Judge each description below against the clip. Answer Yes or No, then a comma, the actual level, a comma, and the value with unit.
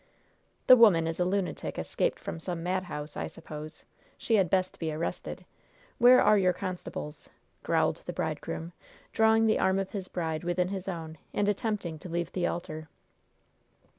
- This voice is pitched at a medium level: Yes, medium, 180 Hz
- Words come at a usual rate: Yes, average, 165 wpm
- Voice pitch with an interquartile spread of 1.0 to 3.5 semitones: Yes, average, 3.2 semitones